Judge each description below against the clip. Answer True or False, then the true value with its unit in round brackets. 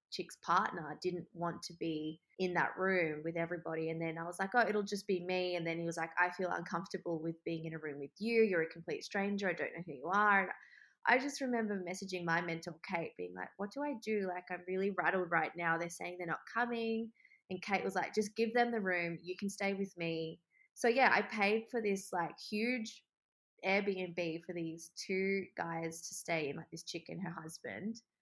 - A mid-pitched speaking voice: True (180 Hz)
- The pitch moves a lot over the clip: False (3.4 semitones)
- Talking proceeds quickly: True (230 wpm)